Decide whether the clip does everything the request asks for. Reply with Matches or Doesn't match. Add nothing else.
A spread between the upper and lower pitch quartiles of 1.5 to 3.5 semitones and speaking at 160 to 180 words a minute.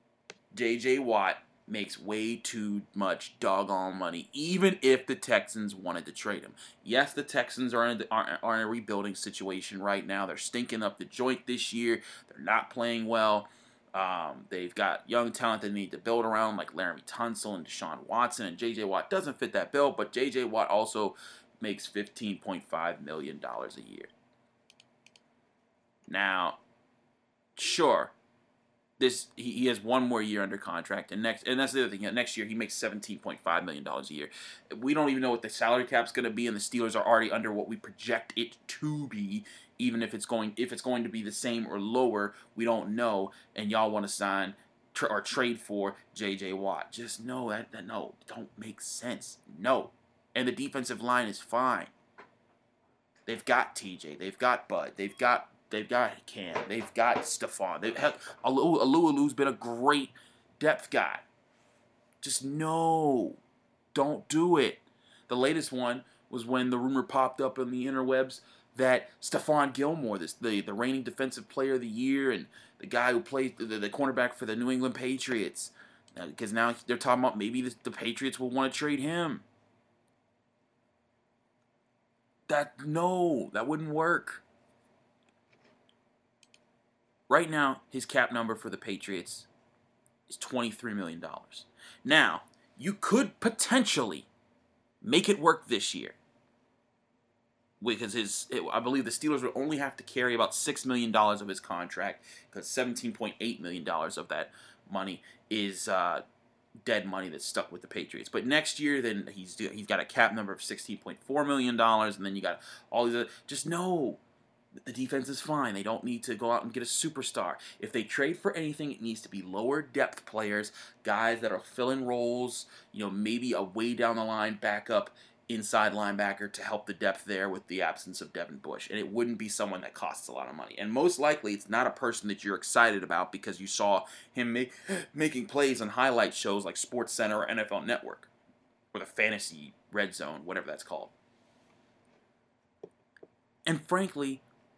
Matches